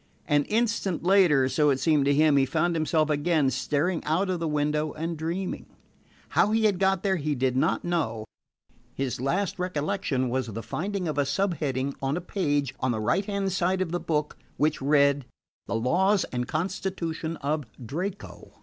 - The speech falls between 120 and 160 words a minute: No, average, 180 wpm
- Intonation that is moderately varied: Yes, average, 4.7 semitones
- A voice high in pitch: No, medium, 155 Hz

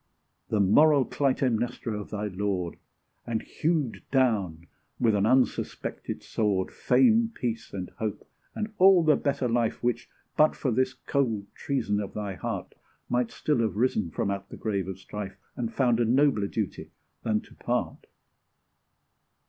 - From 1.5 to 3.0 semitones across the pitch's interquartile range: No, average, 4.3 semitones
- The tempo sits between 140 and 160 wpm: Yes, average, 150 wpm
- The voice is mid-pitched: No, low, 115 Hz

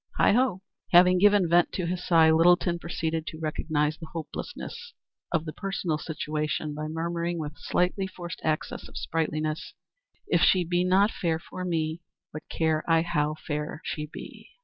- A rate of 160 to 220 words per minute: Yes, average, 165 wpm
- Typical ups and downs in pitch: No, narrow, 2.3 semitones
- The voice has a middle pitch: Yes, medium, 165 Hz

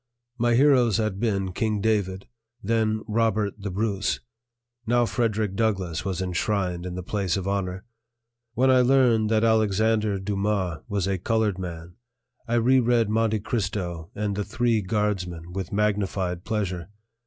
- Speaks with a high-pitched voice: No, low, 105 Hz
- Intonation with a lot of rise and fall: No, average, 3.0 semitones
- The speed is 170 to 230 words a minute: No, average, 145 wpm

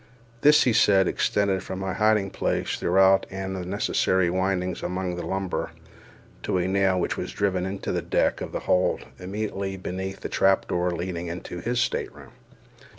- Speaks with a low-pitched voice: Yes, very low, 95 Hz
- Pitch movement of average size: No, narrow, 1.2 semitones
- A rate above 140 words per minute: Yes, average, 170 wpm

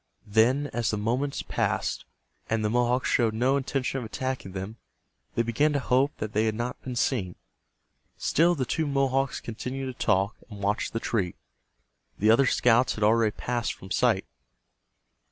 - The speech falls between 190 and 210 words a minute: No, average, 170 wpm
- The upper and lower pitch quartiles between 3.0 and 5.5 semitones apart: Yes, average, 3.4 semitones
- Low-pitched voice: Yes, low, 120 Hz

